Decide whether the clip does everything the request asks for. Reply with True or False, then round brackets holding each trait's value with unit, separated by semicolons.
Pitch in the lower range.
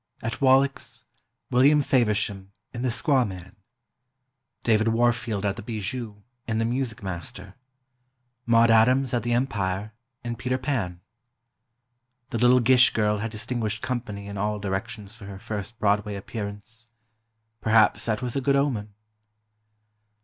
True (115 Hz)